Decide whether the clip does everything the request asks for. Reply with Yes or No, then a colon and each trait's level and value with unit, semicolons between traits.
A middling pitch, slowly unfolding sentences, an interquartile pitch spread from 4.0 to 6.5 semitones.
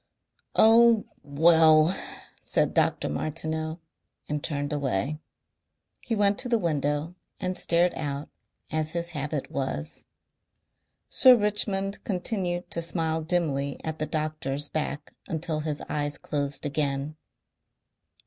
No: medium, 155 Hz; slow, 115 wpm; average, 3.2 semitones